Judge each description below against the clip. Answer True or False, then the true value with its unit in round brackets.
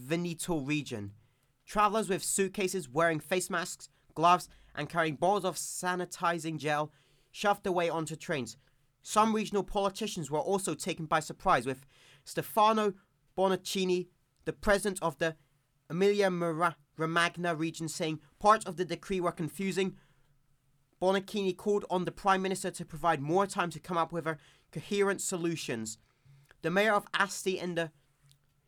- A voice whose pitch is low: False (170 Hz)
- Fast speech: False (140 wpm)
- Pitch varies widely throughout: False (4.4 semitones)